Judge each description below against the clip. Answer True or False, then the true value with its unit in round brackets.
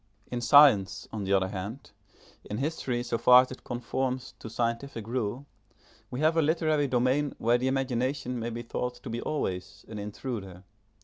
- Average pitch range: True (3.1 semitones)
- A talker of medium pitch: False (120 Hz)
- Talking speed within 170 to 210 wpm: True (175 wpm)